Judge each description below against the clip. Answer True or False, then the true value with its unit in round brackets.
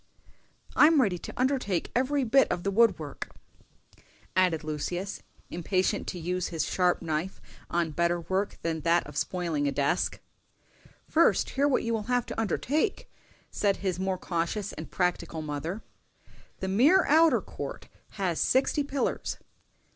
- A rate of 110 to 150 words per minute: True (145 wpm)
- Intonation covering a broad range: True (5.9 semitones)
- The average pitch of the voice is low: False (185 Hz)